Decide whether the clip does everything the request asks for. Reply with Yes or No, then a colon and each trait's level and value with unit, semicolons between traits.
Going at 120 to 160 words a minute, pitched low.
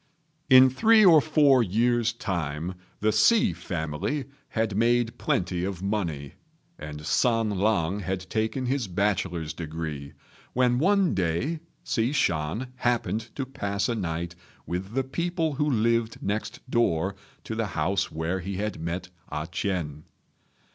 Yes: average, 140 wpm; low, 105 Hz